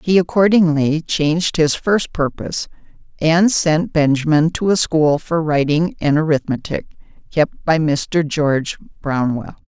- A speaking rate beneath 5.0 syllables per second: Yes, 4.2 syllables/s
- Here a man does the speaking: No, female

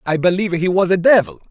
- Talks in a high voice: No, medium, 180 Hz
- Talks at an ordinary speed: No, fast, 240 wpm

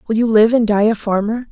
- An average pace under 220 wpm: No, fast, 275 wpm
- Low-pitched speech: No, high, 220 Hz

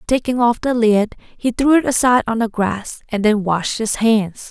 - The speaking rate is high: Yes, fast, 215 wpm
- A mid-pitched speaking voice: No, high, 225 Hz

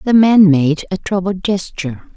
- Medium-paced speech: Yes, average, 165 wpm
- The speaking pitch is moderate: Yes, medium, 180 Hz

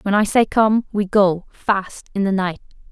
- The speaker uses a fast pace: No, average, 165 wpm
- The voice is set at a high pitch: Yes, high, 200 Hz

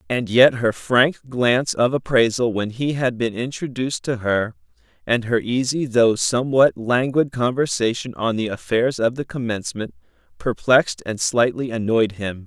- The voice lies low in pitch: Yes, low, 120 Hz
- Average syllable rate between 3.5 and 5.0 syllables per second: Yes, 4.7 syllables/s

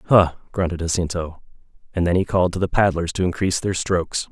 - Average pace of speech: Yes, average, 195 wpm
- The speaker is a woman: No, male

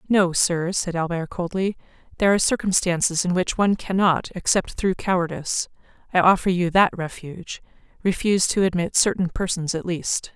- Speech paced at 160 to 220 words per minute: No, average, 145 wpm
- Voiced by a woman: Yes, female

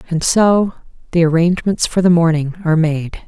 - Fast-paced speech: No, average, 165 wpm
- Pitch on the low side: No, medium, 170 Hz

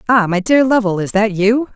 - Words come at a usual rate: No, fast, 240 wpm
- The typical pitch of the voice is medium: No, high, 215 Hz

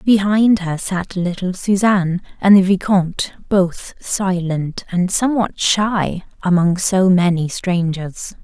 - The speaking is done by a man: No, female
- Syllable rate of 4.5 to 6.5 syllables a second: No, 3.7 syllables/s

